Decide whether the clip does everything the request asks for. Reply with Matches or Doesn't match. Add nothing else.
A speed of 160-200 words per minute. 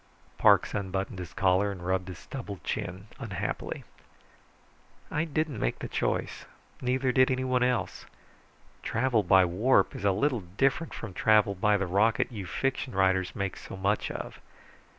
Doesn't match